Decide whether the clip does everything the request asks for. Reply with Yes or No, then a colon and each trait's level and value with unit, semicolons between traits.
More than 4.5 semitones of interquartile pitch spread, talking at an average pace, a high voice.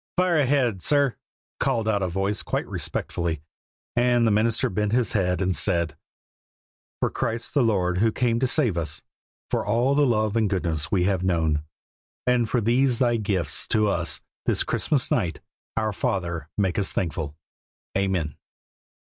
No: average, 4.9 semitones; average, 160 wpm; low, 105 Hz